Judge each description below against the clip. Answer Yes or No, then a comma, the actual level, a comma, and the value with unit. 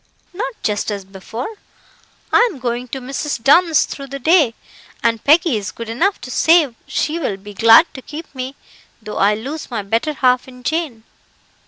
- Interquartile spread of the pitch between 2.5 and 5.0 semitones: No, wide, 5.6 semitones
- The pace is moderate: Yes, average, 180 wpm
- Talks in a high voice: Yes, very high, 255 Hz